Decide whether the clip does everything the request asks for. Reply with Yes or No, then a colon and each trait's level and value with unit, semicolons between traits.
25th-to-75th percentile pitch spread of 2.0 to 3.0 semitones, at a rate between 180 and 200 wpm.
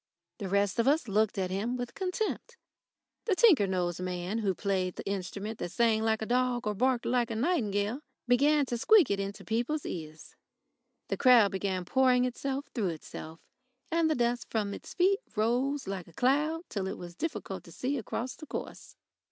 No: average, 5.2 semitones; average, 185 wpm